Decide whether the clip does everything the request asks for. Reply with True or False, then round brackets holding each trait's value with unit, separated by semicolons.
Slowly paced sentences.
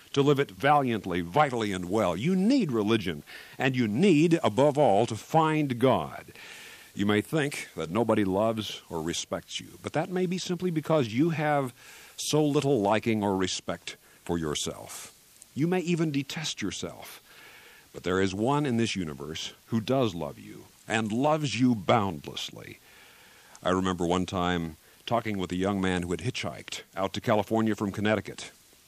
False (165 wpm)